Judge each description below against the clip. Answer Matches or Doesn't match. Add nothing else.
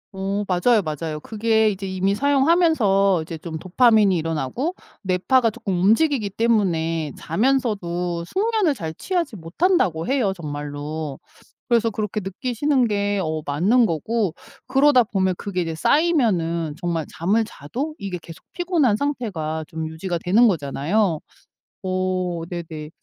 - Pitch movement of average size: Doesn't match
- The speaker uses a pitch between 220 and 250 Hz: Doesn't match